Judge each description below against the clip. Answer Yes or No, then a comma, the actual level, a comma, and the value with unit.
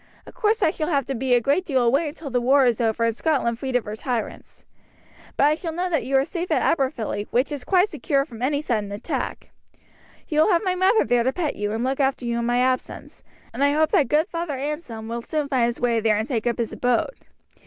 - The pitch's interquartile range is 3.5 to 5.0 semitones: Yes, average, 4.6 semitones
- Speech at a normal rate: No, fast, 250 wpm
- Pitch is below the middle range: No, very high, 265 Hz